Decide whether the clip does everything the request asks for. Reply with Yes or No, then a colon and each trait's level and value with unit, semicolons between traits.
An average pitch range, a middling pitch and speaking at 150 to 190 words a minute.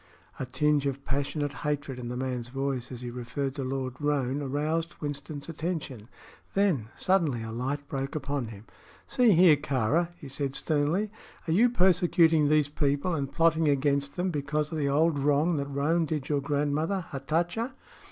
Yes: average, 3.0 semitones; medium, 145 Hz; average, 170 wpm